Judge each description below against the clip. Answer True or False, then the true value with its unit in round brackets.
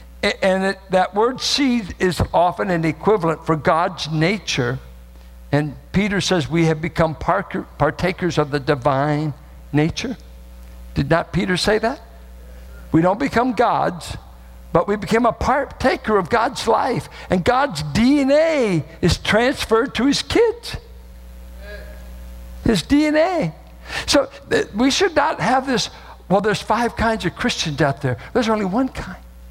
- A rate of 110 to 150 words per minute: True (140 wpm)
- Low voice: False (180 Hz)